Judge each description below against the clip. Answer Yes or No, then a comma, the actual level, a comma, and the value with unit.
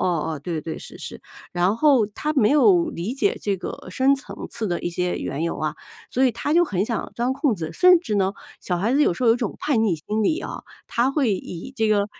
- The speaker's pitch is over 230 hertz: No, high, 220 Hz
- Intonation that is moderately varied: No, wide, 7.2 semitones